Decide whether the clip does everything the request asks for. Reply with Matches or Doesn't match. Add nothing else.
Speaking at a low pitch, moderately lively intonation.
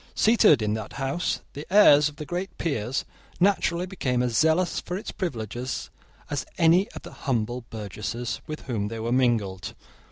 Doesn't match